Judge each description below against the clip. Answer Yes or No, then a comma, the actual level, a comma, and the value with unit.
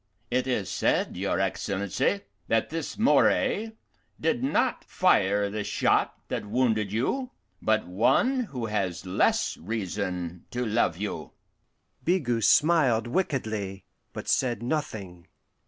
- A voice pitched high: No, low, 110 Hz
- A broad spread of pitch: Yes, wide, 6.4 semitones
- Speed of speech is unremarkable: No, slow, 120 wpm